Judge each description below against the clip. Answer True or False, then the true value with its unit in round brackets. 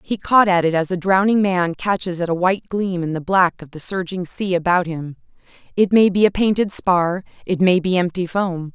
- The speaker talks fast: True (220 wpm)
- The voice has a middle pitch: True (180 Hz)